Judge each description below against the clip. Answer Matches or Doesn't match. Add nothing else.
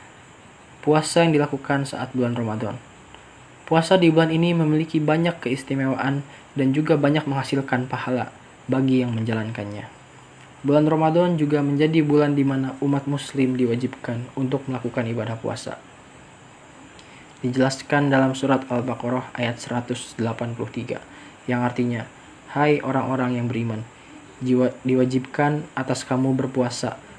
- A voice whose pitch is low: Matches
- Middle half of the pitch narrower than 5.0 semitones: Matches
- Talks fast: Doesn't match